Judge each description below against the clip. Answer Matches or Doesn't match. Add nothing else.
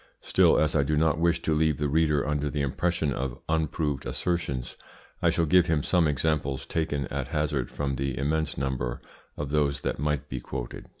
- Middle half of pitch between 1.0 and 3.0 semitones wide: Matches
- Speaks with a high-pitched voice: Doesn't match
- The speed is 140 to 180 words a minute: Doesn't match